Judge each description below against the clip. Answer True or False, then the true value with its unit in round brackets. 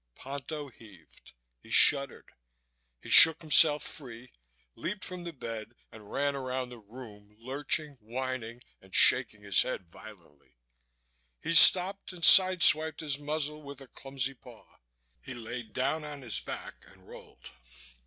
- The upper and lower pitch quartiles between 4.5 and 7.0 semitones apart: True (4.8 semitones)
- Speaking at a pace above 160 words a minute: False (140 wpm)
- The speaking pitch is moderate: False (130 Hz)